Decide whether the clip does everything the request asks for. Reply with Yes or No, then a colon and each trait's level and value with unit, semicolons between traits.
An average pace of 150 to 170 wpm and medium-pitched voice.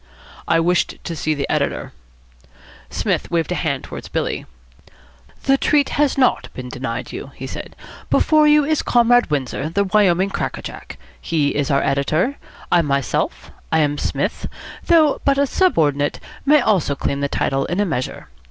Yes: average, 165 wpm; medium, 170 Hz